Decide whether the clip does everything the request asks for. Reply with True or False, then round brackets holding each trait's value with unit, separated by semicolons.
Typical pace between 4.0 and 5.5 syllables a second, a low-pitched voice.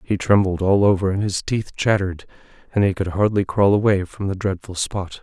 True (5.4 syllables/s; 95 Hz)